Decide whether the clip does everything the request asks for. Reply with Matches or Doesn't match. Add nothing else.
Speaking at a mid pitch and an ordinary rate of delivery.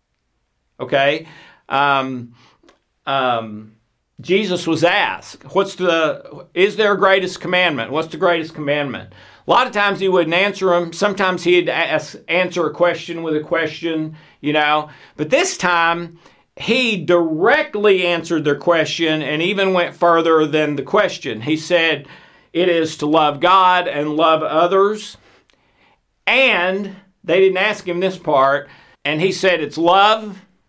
Matches